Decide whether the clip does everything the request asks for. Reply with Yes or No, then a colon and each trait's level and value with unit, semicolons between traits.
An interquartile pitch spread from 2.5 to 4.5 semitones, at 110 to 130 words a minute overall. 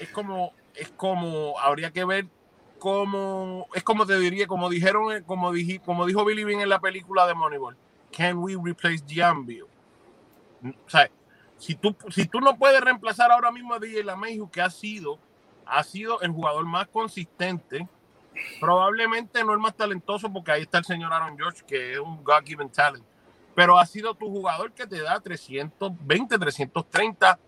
No: average, 4.2 semitones; average, 175 wpm